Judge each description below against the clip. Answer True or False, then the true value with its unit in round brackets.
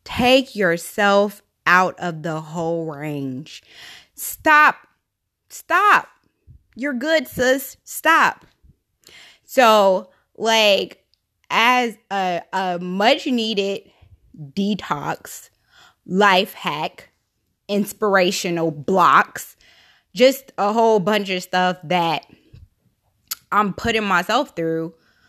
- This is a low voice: False (200 Hz)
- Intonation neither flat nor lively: True (4.9 semitones)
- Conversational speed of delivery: False (85 wpm)